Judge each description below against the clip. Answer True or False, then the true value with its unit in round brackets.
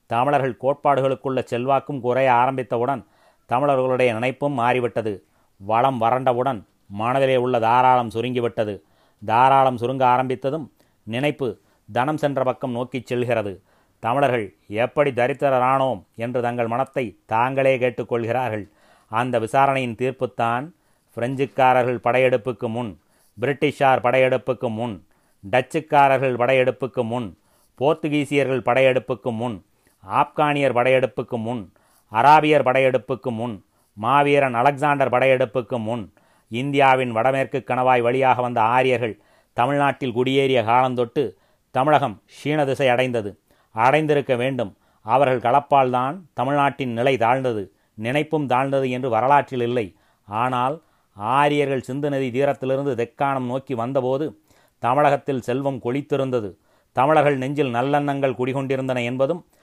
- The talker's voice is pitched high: False (130 Hz)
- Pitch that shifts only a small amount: True (2.3 semitones)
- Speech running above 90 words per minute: True (100 wpm)